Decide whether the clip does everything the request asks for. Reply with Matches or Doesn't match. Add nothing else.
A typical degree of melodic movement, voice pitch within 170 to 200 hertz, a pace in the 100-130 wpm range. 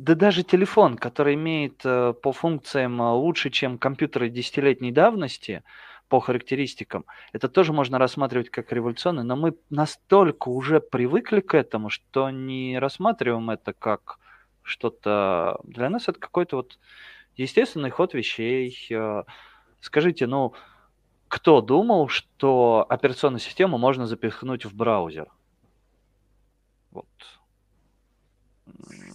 Doesn't match